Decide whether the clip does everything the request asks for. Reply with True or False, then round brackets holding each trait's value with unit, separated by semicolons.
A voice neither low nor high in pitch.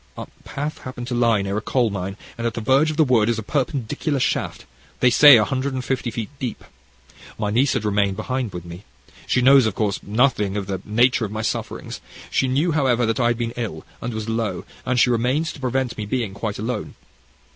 False (120 Hz)